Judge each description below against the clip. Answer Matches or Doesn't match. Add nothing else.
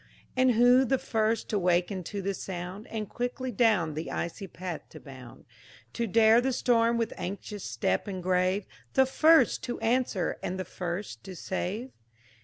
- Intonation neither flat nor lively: Matches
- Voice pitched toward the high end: Matches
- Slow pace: Doesn't match